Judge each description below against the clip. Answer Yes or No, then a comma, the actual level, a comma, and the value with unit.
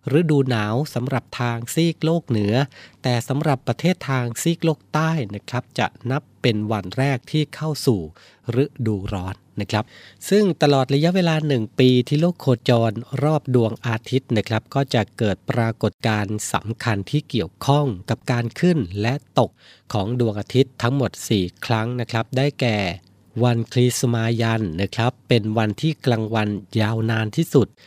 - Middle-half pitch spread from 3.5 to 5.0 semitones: Yes, average, 4.0 semitones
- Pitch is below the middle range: Yes, low, 120 Hz